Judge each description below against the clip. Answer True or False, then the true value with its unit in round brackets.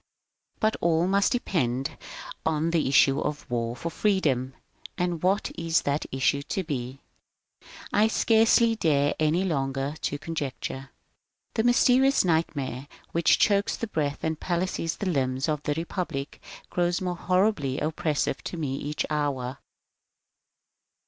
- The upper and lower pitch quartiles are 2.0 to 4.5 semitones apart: False (4.9 semitones)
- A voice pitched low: False (160 Hz)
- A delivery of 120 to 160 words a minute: True (135 wpm)